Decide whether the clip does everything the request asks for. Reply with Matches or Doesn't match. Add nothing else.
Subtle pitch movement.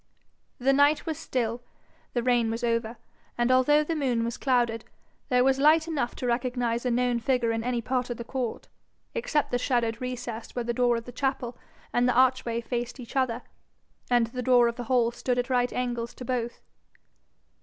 Matches